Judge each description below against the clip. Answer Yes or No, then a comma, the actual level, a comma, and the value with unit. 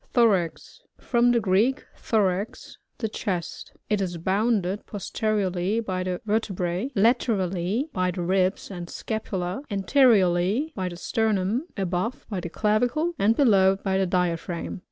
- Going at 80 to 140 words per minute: Yes, slow, 135 wpm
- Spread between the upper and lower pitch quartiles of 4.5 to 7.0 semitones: No, average, 3.6 semitones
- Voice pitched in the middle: No, high, 195 Hz